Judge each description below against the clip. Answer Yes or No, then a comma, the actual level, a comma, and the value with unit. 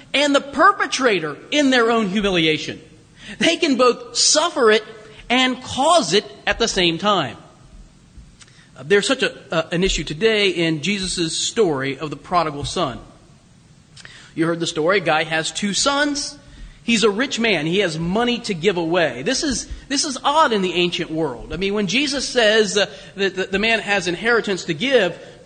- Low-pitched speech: No, high, 205 Hz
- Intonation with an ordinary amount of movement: No, wide, 6.4 semitones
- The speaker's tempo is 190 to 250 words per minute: No, average, 175 wpm